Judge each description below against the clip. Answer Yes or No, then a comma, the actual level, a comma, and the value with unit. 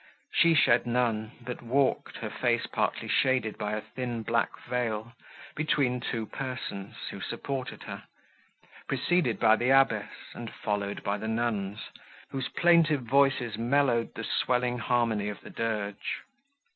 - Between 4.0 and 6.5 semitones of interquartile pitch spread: No, average, 3.1 semitones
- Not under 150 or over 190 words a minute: No, slow, 135 wpm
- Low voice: Yes, low, 120 Hz